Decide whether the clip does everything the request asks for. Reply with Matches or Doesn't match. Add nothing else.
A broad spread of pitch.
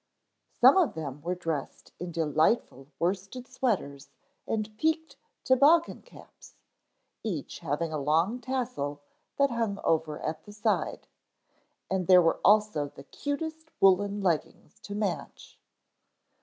Matches